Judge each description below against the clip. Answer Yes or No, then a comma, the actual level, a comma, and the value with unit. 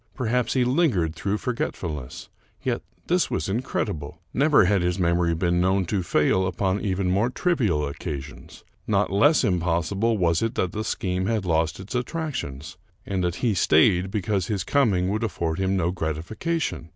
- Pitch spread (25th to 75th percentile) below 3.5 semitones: No, average, 4.8 semitones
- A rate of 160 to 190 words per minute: Yes, average, 170 wpm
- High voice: No, very low, 95 Hz